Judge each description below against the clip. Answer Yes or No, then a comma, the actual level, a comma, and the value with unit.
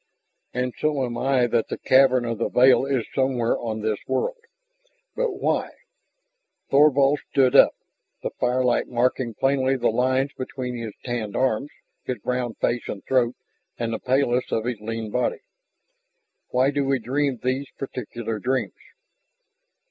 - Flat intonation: Yes, narrow, 2.2 semitones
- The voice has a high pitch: No, low, 125 Hz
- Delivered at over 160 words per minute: No, average, 150 wpm